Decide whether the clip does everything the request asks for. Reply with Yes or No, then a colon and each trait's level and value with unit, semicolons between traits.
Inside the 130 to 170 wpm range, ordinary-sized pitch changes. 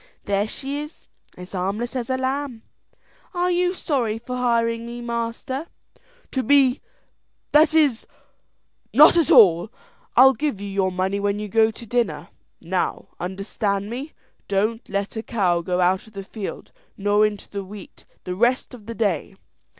Yes: average, 160 wpm; average, 4.6 semitones